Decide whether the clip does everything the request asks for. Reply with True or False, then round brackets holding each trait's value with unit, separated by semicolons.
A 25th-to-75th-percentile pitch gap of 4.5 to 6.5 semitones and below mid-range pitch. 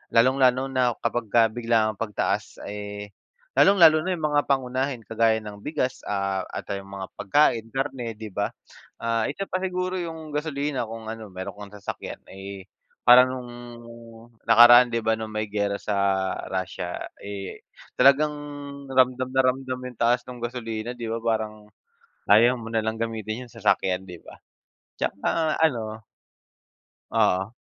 False (3.6 semitones; 115 Hz)